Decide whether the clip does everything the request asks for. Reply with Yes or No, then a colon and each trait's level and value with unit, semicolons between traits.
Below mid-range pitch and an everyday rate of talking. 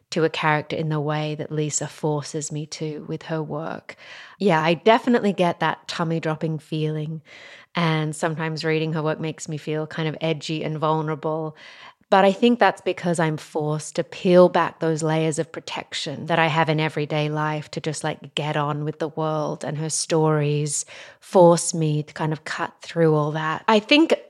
No: medium, 160 Hz; average, 190 wpm